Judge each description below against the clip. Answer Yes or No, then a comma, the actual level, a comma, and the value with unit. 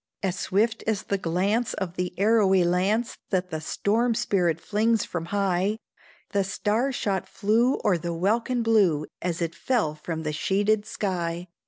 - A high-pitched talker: Yes, high, 195 Hz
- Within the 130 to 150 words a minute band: No, average, 160 wpm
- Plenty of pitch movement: No, average, 3.9 semitones